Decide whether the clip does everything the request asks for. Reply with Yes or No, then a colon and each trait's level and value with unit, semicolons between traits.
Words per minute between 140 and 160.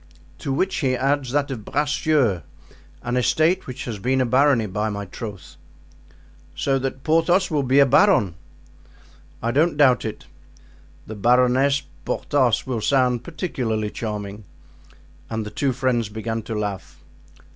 Yes: average, 145 wpm